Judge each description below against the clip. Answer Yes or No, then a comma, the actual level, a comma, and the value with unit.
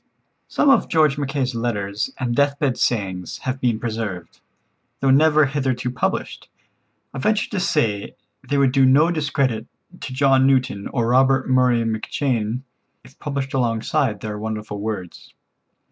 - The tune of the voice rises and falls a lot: No, average, 3.9 semitones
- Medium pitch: No, low, 130 Hz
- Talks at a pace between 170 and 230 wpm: No, average, 140 wpm